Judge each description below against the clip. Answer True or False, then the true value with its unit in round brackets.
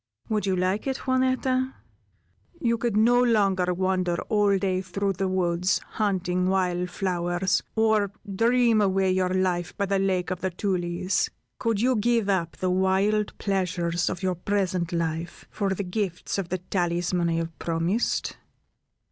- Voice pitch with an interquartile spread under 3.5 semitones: True (2.5 semitones)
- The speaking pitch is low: False (190 Hz)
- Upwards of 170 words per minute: False (155 wpm)